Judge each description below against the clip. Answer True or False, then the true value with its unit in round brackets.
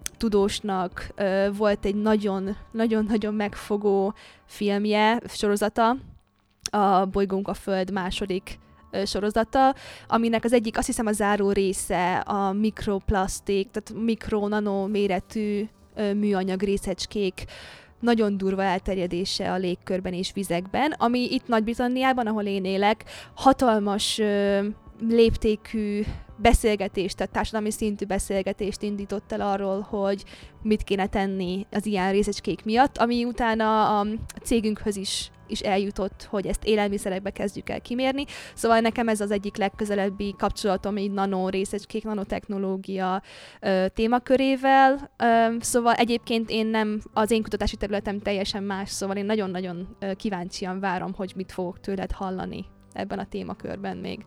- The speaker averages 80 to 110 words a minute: False (125 wpm)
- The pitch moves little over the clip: True (2.2 semitones)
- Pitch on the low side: False (205 Hz)